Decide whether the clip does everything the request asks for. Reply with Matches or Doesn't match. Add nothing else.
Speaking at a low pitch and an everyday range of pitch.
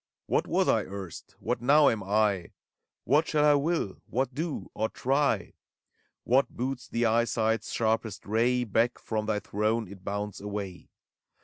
Matches